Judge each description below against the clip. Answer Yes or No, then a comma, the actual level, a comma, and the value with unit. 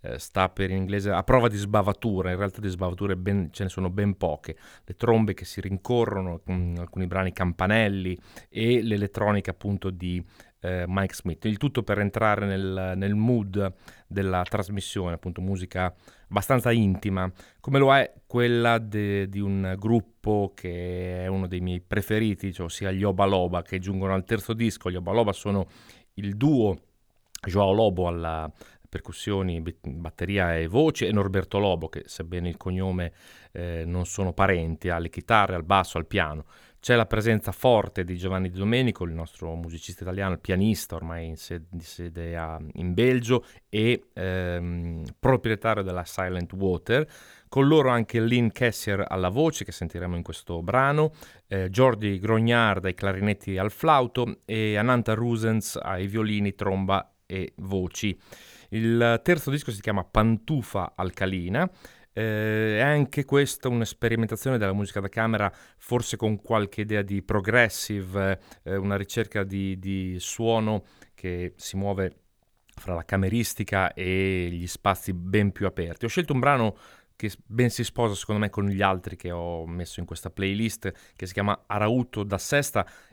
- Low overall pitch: Yes, low, 100 Hz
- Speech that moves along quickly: No, average, 155 wpm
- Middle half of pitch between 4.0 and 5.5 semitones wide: No, average, 3.5 semitones